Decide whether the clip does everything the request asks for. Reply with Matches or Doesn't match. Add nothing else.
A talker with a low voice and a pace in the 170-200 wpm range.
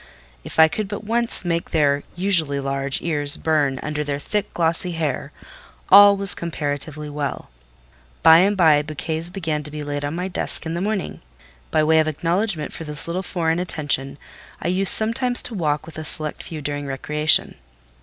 Doesn't match